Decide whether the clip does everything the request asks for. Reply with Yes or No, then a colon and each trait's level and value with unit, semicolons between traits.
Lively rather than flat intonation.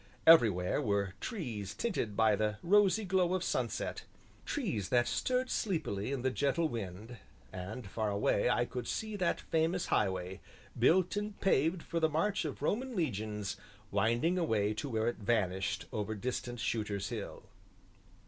Yes: wide, 8.6 semitones